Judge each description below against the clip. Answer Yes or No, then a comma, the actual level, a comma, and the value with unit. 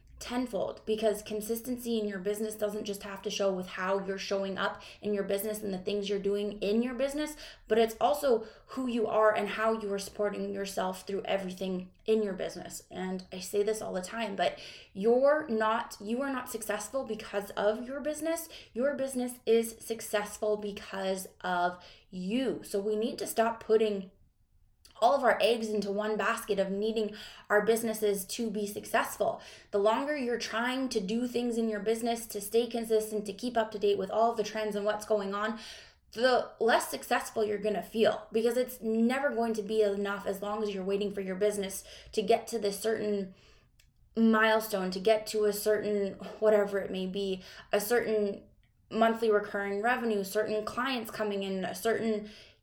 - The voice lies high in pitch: Yes, high, 215 Hz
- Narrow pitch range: Yes, narrow, 2.1 semitones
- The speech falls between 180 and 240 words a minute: Yes, average, 185 wpm